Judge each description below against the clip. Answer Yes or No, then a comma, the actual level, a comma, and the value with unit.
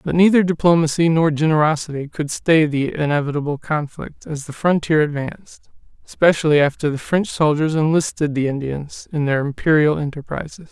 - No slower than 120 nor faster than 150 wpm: Yes, average, 145 wpm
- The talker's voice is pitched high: No, medium, 155 Hz